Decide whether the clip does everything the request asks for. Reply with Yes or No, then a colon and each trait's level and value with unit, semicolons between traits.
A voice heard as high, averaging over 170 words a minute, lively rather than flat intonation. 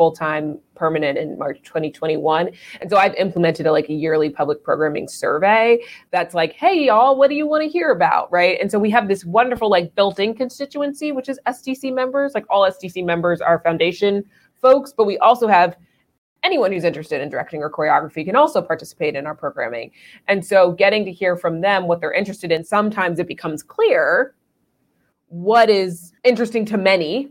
Yes: high, 195 Hz; average, 190 wpm; wide, 6.2 semitones